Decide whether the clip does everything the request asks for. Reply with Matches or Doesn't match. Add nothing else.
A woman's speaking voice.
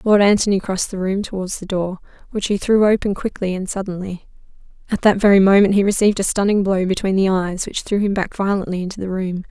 Matches